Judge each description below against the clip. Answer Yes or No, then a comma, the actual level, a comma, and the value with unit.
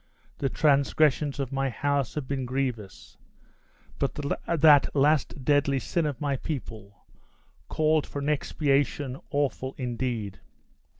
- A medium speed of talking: No, slow, 120 wpm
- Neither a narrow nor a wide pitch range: No, narrow, 2.2 semitones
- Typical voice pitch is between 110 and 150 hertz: Yes, medium, 140 Hz